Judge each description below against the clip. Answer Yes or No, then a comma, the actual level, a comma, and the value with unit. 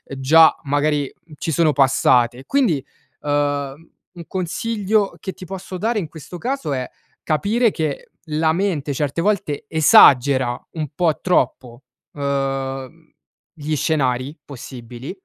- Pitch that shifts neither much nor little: Yes, average, 4.6 semitones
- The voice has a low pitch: No, medium, 150 Hz